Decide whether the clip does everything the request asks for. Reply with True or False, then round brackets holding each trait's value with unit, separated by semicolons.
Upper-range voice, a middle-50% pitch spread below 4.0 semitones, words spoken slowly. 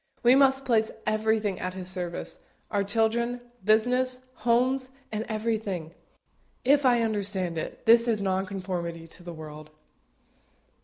False (215 Hz; 4.4 semitones; 125 wpm)